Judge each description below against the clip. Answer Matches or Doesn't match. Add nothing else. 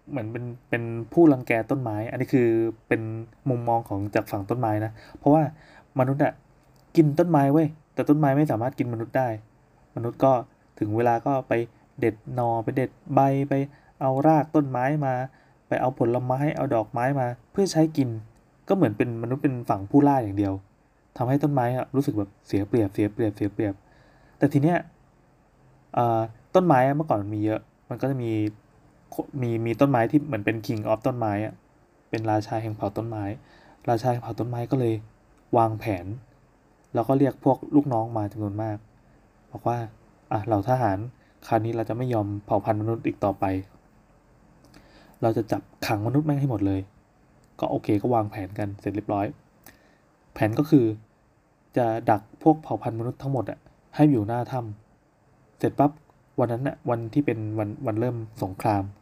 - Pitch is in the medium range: Doesn't match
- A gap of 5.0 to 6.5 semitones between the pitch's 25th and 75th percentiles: Doesn't match